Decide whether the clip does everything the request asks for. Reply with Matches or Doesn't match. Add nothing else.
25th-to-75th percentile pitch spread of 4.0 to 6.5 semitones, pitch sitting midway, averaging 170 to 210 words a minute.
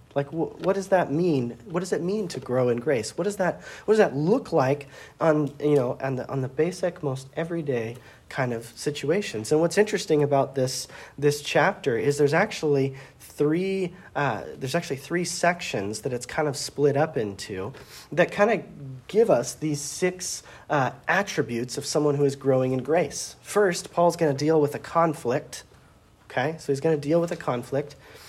Matches